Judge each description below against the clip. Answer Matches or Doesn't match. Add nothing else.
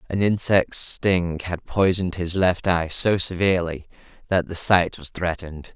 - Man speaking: Matches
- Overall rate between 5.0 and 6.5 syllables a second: Doesn't match